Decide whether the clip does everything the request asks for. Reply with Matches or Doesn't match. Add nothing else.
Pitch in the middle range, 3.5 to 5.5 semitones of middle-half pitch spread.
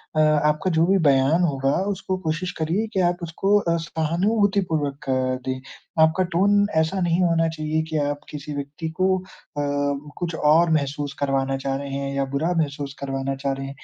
Matches